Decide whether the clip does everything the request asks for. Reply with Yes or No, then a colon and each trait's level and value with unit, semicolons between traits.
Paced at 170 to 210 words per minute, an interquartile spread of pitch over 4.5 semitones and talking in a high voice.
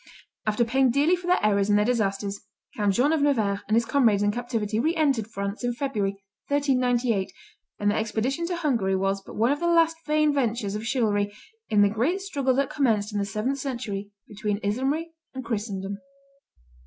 Yes: average, 190 wpm; average, 5.2 semitones; high, 230 Hz